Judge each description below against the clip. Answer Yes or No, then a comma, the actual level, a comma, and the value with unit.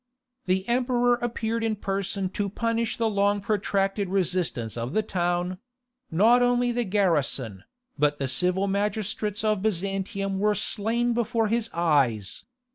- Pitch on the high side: Yes, high, 200 Hz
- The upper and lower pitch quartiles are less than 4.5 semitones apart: Yes, average, 3.8 semitones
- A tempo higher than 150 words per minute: No, slow, 135 wpm